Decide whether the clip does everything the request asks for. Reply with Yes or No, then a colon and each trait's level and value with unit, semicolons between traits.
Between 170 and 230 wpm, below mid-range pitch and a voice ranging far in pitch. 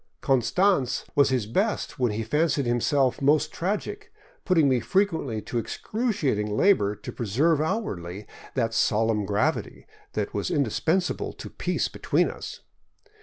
No: slow, 135 wpm; low, 130 Hz; wide, 6.9 semitones